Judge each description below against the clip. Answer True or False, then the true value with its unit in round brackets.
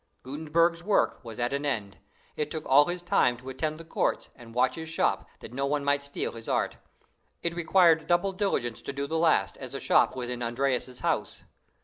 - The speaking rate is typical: False (210 wpm)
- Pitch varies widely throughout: False (4.6 semitones)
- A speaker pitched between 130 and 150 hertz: True (140 Hz)